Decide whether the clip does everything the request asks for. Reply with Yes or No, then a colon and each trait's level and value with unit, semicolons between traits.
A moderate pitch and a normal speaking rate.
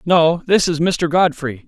Yes: medium, 165 Hz; average, 180 wpm